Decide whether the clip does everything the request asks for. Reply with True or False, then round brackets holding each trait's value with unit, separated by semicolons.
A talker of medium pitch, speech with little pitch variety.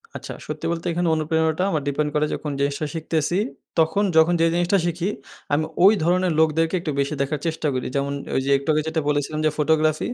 True (160 Hz; 1.9 semitones)